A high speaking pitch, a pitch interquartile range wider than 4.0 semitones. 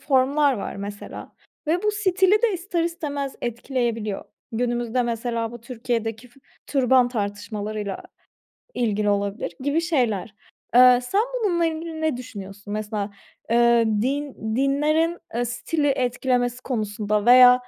Yes: high, 245 Hz; average, 4.7 semitones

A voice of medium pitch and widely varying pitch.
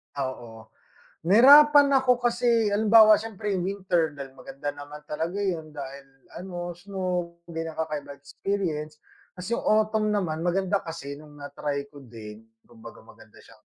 Yes: medium, 175 Hz; wide, 6.1 semitones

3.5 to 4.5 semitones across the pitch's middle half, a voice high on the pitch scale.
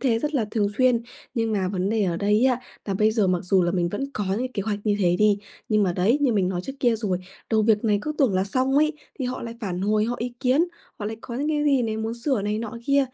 Yes: average, 3.9 semitones; high, 220 Hz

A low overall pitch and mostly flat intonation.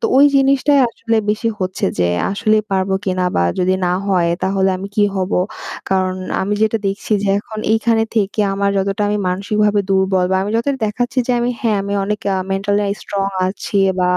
No: high, 200 Hz; narrow, 2.3 semitones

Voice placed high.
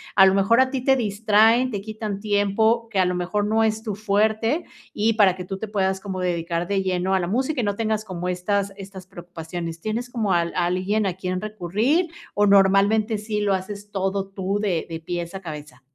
Yes: high, 200 Hz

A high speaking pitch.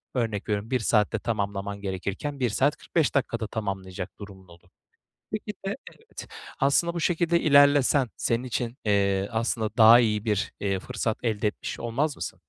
No: low, 115 Hz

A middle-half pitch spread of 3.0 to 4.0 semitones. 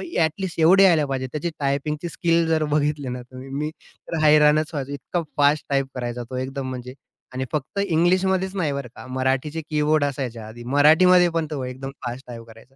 Yes: average, 3.7 semitones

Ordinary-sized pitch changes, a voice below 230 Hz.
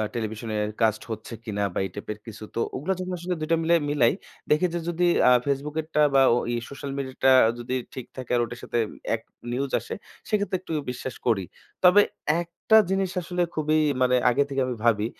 No: wide, 6.0 semitones; low, 135 Hz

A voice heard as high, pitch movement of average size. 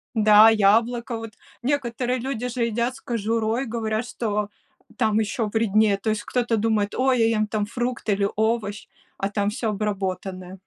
No: high, 220 Hz; narrow, 2.2 semitones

